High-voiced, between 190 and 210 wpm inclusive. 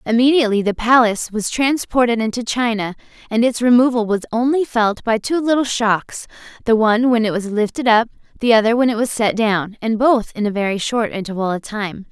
Yes: high, 230 Hz; average, 200 wpm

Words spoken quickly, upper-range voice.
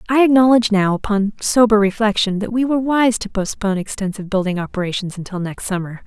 No: average, 180 wpm; high, 210 Hz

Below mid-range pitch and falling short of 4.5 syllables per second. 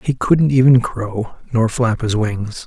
Yes: low, 115 Hz; 3.7 syllables/s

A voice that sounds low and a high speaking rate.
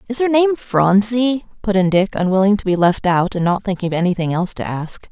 No: high, 200 Hz; fast, 235 wpm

